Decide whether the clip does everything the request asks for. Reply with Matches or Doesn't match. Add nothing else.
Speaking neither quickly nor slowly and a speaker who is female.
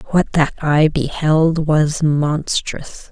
Doesn't match